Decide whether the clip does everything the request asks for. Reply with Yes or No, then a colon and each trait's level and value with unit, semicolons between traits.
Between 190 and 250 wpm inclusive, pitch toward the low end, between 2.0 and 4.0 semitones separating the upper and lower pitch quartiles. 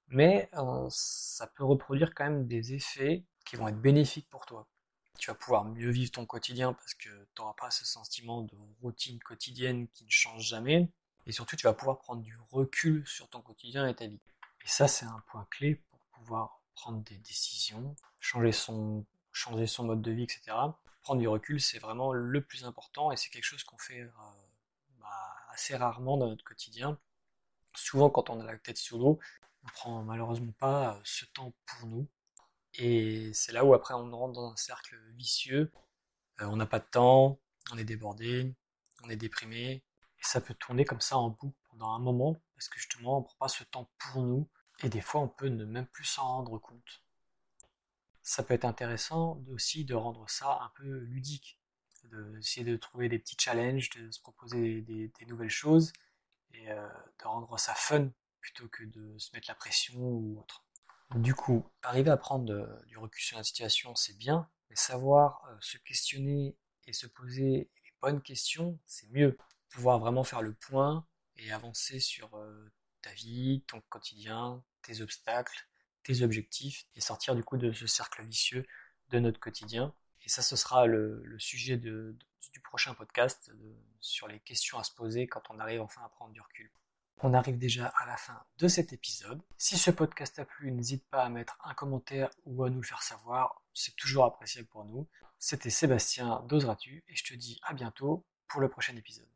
Yes: average, 195 wpm; low, 125 Hz; average, 3.3 semitones